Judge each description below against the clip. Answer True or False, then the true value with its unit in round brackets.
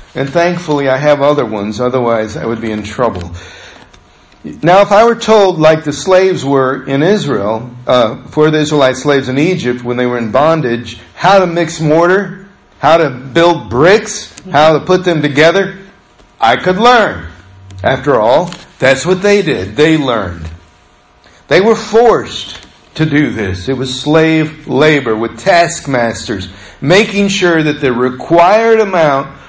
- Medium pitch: True (150 Hz)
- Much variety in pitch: True (6.7 semitones)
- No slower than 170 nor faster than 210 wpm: False (155 wpm)